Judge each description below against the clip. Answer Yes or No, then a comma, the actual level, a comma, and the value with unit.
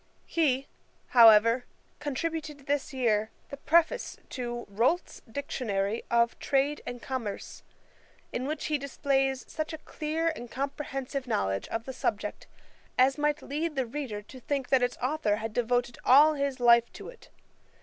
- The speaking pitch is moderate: No, very high, 265 Hz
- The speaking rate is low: No, average, 150 wpm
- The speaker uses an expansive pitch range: No, average, 3.6 semitones